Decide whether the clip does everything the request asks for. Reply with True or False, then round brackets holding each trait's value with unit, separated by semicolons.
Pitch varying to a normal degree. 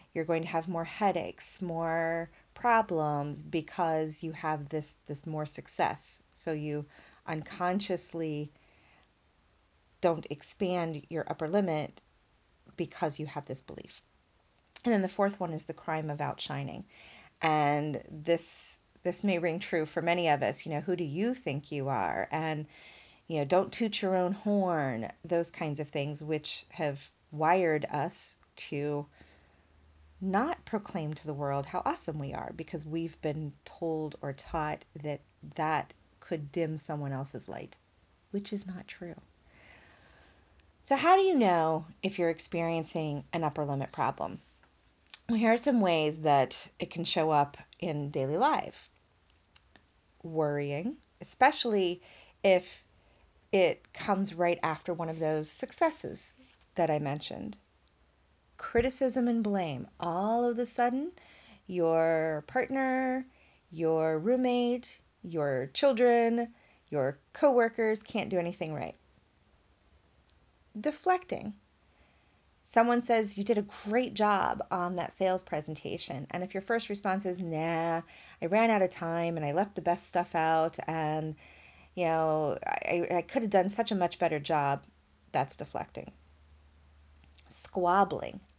True (4.6 semitones)